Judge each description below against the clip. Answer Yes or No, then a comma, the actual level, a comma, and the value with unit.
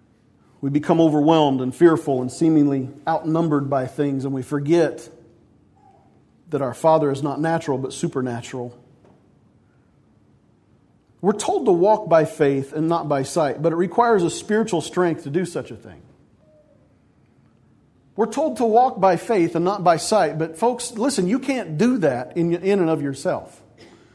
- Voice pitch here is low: No, medium, 160 Hz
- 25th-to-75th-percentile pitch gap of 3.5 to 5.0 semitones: Yes, average, 4.7 semitones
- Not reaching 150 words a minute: No, average, 155 wpm